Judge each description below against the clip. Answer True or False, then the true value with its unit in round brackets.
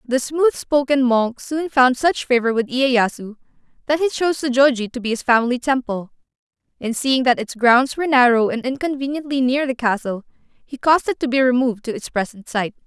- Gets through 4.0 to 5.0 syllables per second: False (5.4 syllables/s)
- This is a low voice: False (255 Hz)